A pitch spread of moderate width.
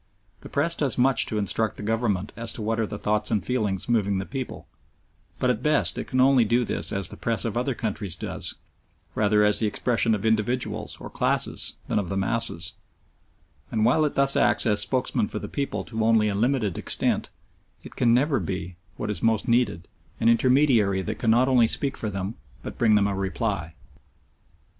Yes: average, 3.3 semitones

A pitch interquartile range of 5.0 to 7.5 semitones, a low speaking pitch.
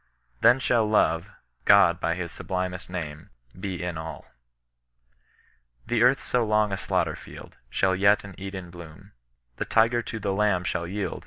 No: average, 3.4 semitones; very low, 95 Hz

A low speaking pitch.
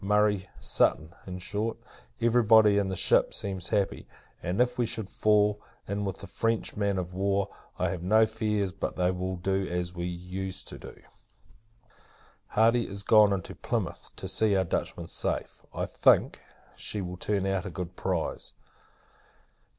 Yes: low, 100 Hz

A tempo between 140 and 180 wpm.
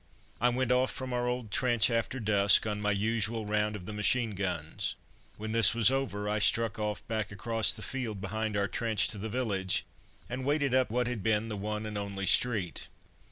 No: fast, 205 wpm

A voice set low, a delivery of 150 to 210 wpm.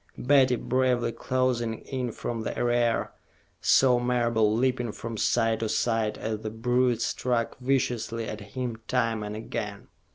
No: low, 120 Hz; average, 140 wpm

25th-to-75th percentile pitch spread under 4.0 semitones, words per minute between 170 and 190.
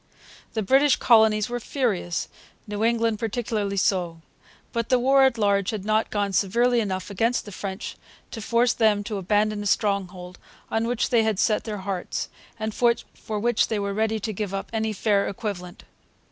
Yes: narrow, 2.6 semitones; average, 175 wpm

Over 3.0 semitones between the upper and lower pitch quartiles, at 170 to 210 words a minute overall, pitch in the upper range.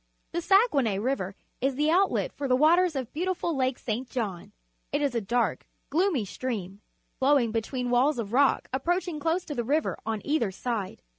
Yes: average, 5.2 semitones; average, 175 wpm; very high, 265 Hz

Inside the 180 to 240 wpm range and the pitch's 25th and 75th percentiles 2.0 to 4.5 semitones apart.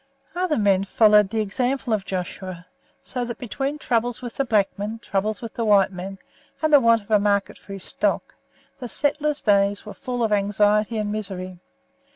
Yes: average, 190 wpm; average, 3.5 semitones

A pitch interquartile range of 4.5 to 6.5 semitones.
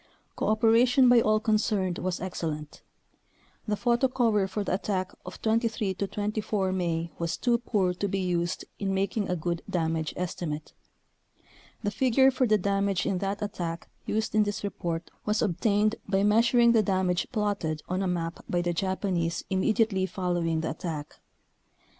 No: average, 3.5 semitones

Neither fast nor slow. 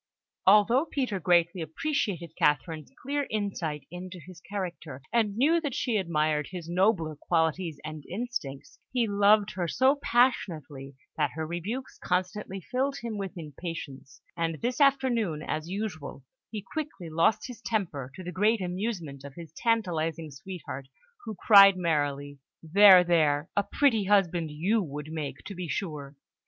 Yes: average, 145 wpm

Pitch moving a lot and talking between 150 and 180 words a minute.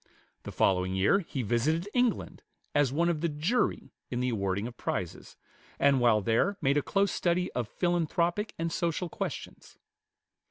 Yes: wide, 6.7 semitones; average, 160 wpm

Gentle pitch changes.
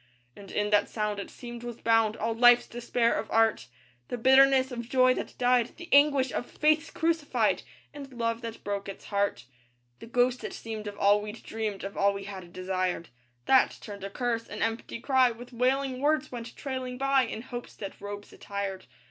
No: average, 3.9 semitones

